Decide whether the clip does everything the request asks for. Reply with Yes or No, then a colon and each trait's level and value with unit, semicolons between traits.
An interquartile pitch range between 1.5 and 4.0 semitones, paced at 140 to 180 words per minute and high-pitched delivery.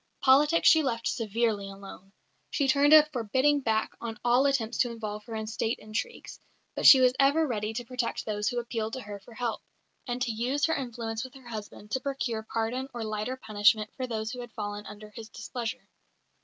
No: average, 3.2 semitones; average, 200 wpm; high, 235 Hz